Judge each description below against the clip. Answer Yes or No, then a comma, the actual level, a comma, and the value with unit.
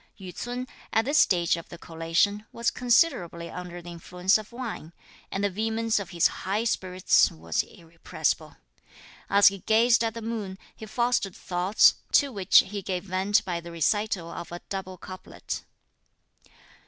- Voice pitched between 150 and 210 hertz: Yes, high, 190 Hz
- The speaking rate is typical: Yes, average, 160 wpm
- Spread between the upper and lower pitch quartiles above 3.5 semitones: Yes, average, 4.1 semitones